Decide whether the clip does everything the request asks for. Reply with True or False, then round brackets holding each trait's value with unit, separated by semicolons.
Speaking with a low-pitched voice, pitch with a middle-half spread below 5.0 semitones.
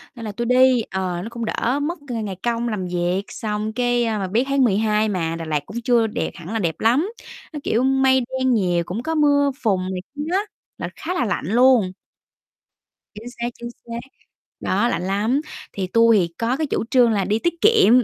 False (230 Hz; 4.6 semitones)